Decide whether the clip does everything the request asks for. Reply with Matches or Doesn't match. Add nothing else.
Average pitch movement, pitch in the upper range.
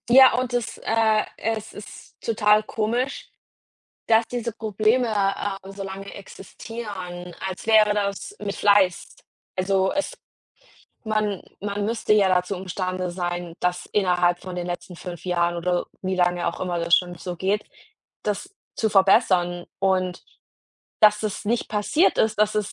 Matches